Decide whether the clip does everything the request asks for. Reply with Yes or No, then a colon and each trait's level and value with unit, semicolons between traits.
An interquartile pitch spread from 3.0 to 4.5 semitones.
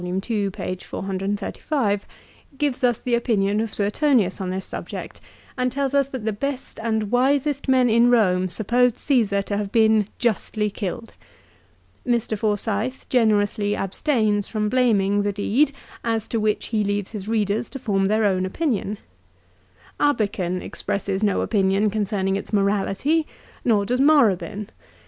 Yes: average, 3.5 semitones